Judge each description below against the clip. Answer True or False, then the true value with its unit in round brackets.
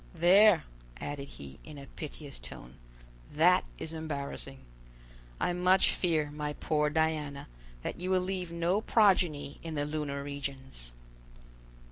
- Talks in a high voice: False (150 Hz)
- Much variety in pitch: False (3.7 semitones)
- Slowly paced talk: True (130 wpm)